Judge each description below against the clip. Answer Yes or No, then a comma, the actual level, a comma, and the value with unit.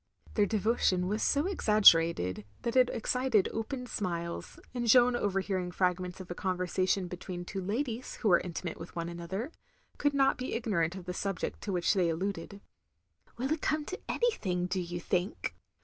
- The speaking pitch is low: No, high, 195 Hz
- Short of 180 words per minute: Yes, average, 170 wpm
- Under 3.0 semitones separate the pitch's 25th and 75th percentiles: No, average, 5.1 semitones